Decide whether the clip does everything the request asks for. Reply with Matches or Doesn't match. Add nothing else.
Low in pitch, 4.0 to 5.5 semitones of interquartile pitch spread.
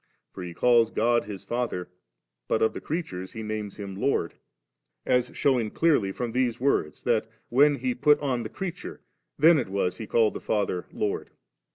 Matches